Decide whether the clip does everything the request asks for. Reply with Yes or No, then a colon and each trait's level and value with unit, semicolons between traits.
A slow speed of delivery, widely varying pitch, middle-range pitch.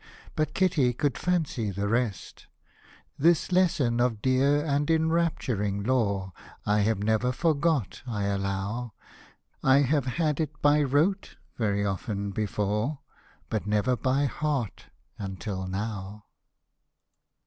No: slow, 115 wpm; wide, 6.2 semitones; low, 120 Hz